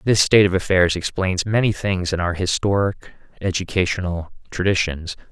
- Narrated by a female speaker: No, male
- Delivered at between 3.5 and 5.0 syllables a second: No, 5.2 syllables/s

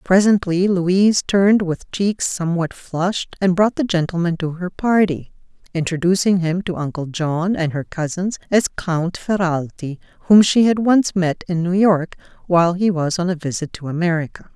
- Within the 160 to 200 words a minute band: Yes, average, 170 wpm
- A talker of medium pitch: Yes, medium, 180 Hz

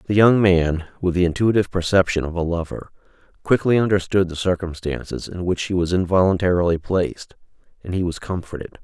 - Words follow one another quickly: No, average, 165 wpm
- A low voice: Yes, very low, 90 Hz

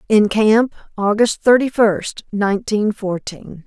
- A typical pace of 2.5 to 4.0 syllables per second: Yes, 3.7 syllables/s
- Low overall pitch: No, high, 210 Hz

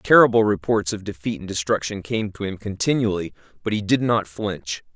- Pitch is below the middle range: Yes, low, 100 Hz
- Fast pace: No, average, 180 wpm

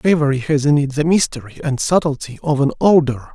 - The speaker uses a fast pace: No, average, 195 wpm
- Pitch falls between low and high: Yes, medium, 145 Hz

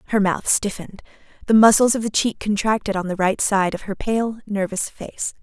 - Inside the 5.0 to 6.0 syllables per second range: Yes, 5.2 syllables/s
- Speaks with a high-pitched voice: Yes, high, 205 Hz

